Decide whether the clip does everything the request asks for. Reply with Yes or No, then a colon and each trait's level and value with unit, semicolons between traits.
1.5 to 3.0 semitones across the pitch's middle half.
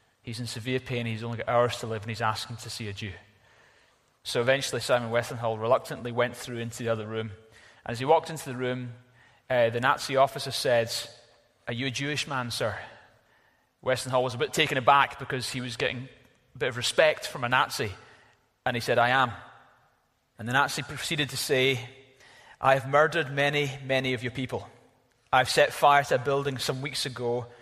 Yes: narrow, 2.5 semitones